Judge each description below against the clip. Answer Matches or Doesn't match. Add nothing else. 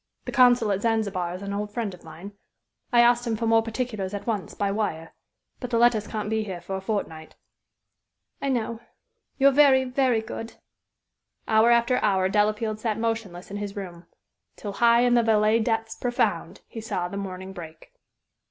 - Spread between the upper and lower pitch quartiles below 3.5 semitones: Matches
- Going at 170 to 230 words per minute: Matches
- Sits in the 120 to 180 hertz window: Doesn't match